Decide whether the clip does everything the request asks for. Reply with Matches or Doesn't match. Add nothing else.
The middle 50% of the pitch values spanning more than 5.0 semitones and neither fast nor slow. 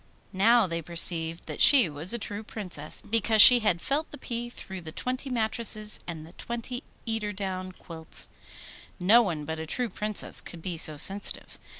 Matches